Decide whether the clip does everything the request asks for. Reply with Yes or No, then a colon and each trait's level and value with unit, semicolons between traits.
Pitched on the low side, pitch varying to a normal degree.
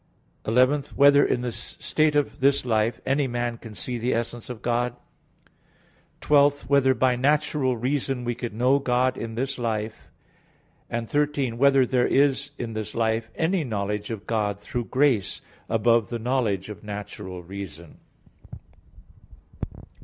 Yes: low, 120 Hz; average, 3.5 semitones